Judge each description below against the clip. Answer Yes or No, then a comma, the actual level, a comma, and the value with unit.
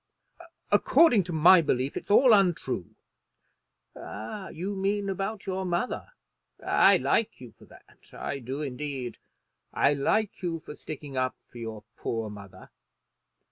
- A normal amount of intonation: No, wide, 7.2 semitones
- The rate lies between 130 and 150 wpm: Yes, slow, 135 wpm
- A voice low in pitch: No, medium, 160 Hz